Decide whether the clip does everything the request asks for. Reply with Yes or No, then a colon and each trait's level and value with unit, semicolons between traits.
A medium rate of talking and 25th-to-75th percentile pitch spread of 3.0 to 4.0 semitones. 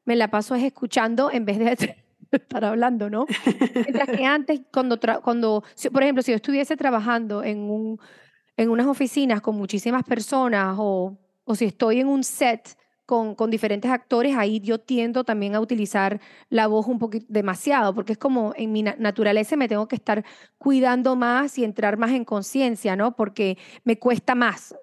Yes: average, 180 wpm; average, 3.3 semitones